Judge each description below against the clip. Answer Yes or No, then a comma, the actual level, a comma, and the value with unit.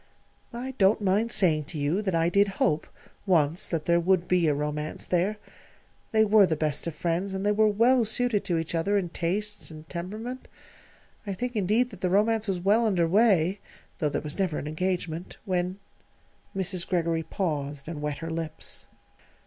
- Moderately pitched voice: Yes, medium, 180 Hz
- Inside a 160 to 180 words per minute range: No, average, 190 wpm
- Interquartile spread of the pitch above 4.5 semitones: No, average, 4.1 semitones